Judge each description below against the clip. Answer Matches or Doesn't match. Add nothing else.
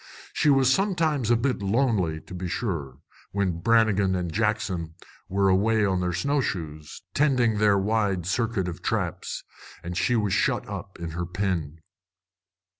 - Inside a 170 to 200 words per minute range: Doesn't match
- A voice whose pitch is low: Matches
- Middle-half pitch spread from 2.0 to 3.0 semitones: Doesn't match